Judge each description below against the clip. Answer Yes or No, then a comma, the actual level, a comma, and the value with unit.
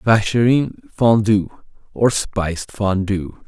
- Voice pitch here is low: Yes, low, 105 Hz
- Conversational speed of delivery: No, slow, 85 wpm